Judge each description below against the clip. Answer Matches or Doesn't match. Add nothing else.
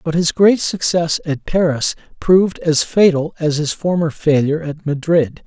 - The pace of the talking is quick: Doesn't match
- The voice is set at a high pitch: Doesn't match